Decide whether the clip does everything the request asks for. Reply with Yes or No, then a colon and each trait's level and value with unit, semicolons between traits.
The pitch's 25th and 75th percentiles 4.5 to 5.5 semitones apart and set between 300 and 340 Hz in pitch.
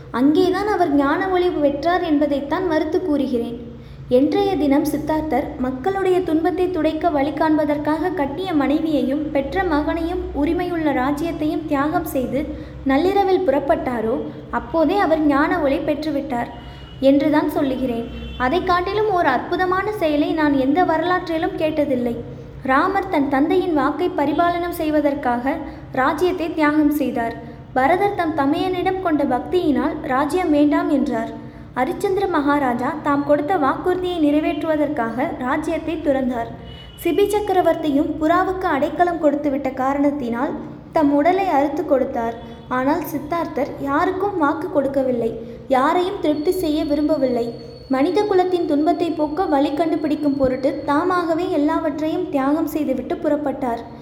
No: average, 3.7 semitones; very high, 305 Hz